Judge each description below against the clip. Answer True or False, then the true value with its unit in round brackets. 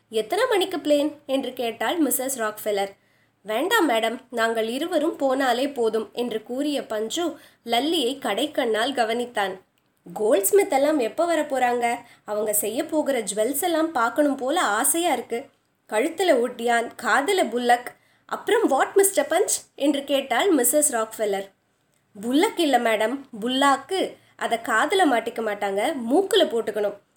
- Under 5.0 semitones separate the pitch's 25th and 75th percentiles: False (5.3 semitones)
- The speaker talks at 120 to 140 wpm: True (125 wpm)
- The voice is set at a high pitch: True (255 Hz)